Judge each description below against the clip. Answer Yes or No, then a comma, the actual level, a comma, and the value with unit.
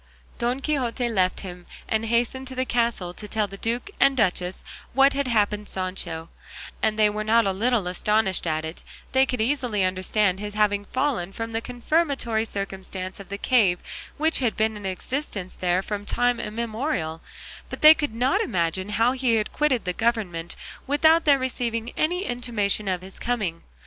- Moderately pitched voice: No, high, 220 Hz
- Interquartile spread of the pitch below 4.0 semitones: No, average, 4.5 semitones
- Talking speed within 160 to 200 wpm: Yes, average, 175 wpm